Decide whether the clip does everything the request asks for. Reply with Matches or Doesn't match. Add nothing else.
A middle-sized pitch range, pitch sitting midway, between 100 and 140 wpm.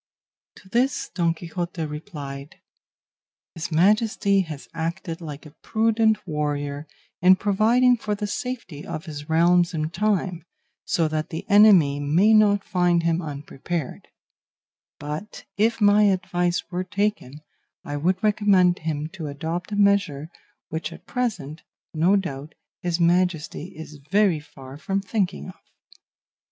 Matches